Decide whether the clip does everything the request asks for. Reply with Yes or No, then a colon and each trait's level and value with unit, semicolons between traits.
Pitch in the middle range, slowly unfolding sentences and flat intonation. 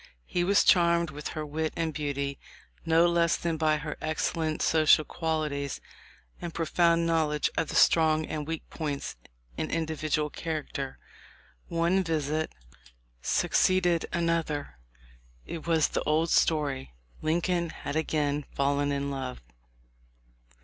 Yes: medium, 155 Hz; slow, 130 wpm; narrow, 2.1 semitones